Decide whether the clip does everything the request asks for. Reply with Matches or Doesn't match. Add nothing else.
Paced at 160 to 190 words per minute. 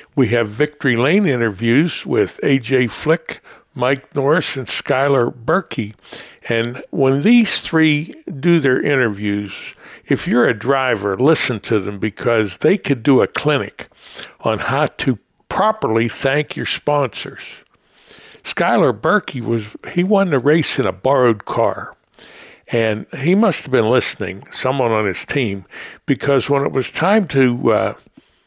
Doesn't match